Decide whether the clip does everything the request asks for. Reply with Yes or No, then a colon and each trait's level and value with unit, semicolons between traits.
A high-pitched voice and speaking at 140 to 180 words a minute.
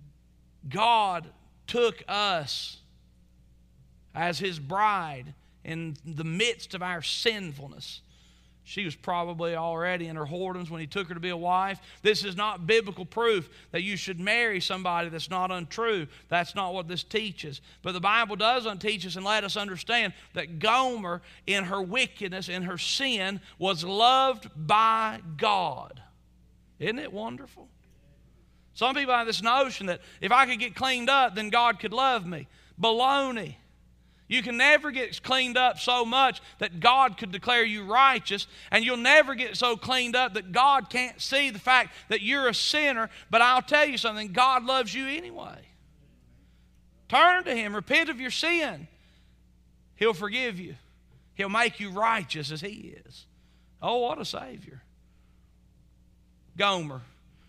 Yes: high, 200 Hz; average, 155 wpm